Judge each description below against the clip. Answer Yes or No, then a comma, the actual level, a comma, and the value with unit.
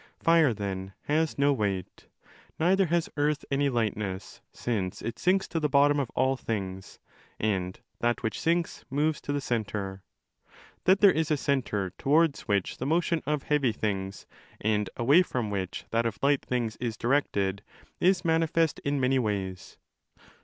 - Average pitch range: No, wide, 6.7 semitones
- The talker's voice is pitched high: No, low, 130 Hz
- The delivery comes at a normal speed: Yes, average, 155 wpm